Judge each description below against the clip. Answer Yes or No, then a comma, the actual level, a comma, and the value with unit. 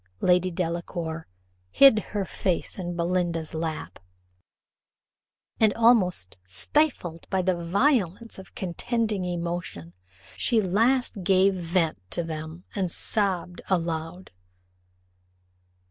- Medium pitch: Yes, medium, 180 Hz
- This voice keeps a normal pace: No, slow, 100 wpm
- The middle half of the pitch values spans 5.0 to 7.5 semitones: No, average, 3.1 semitones